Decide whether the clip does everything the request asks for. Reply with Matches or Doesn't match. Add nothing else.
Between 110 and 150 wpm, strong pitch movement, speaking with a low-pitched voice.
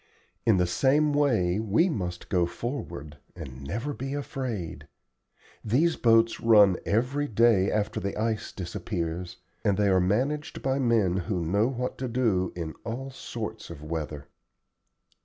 Matches